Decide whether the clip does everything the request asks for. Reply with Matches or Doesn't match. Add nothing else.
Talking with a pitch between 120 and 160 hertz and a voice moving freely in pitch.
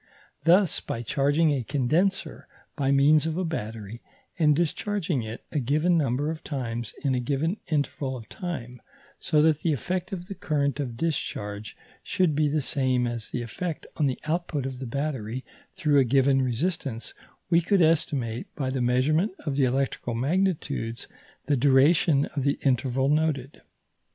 Doesn't match